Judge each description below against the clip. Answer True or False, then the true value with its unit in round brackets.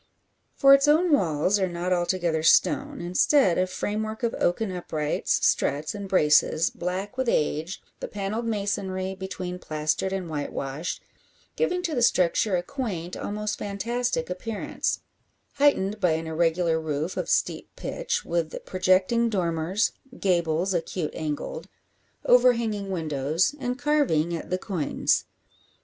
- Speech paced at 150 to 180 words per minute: False (135 wpm)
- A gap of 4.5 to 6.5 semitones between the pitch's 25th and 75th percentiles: True (5.0 semitones)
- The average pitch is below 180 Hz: False (185 Hz)